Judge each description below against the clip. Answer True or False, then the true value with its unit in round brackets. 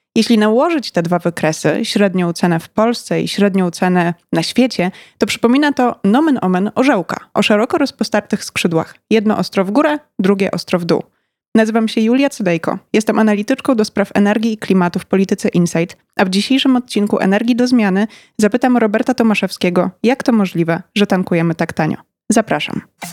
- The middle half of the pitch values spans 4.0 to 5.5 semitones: True (4.4 semitones)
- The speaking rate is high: True (165 wpm)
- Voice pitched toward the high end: True (210 Hz)